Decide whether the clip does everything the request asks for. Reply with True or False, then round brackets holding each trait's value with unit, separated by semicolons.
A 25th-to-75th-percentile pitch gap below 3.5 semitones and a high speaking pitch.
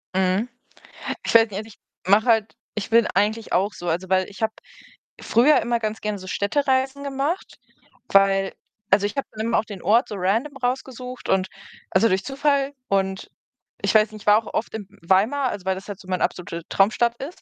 False (4.1 semitones; 215 Hz)